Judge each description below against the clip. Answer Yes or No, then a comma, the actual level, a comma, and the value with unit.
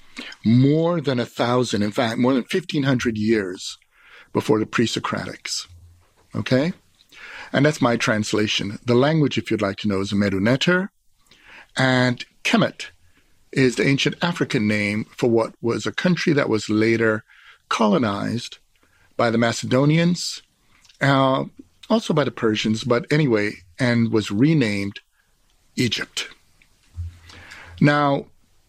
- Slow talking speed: Yes, slow, 125 wpm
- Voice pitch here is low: Yes, low, 120 Hz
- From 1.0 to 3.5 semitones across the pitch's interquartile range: No, average, 5.1 semitones